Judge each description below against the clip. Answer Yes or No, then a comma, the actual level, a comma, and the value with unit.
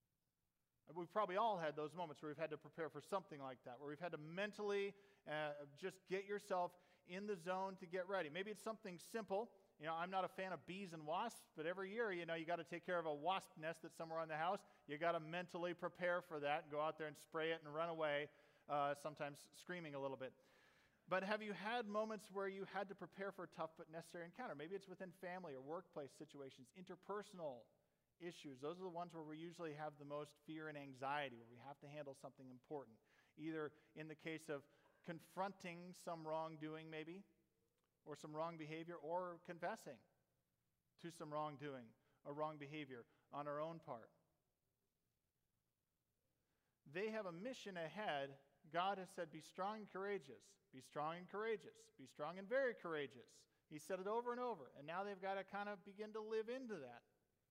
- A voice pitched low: No, medium, 170 Hz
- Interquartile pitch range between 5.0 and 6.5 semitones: No, average, 4.2 semitones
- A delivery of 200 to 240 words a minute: Yes, fast, 205 wpm